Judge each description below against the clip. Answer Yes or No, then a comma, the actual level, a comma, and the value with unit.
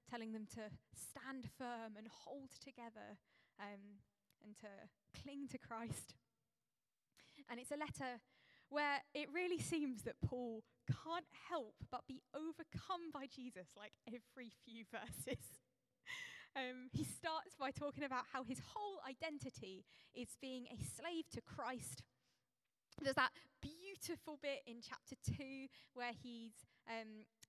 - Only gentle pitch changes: No, average, 4.1 semitones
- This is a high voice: Yes, very high, 260 Hz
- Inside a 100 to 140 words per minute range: Yes, slow, 135 wpm